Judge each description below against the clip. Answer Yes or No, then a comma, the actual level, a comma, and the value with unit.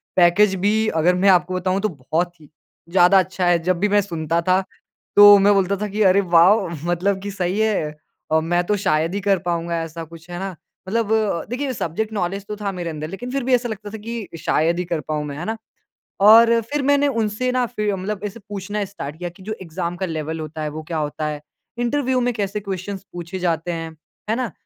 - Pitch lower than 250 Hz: Yes, high, 190 Hz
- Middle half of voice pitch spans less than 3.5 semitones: No, average, 3.8 semitones